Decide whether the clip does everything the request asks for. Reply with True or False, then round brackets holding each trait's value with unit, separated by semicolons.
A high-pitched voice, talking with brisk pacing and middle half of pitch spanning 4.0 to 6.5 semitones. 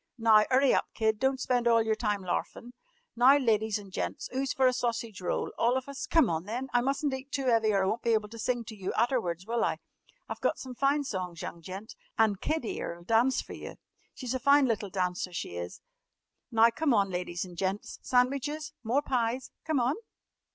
True (230 Hz; 215 wpm; 4.3 semitones)